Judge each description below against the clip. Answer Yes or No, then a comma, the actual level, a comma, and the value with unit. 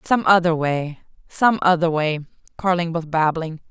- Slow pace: Yes, slow, 130 wpm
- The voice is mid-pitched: Yes, medium, 170 Hz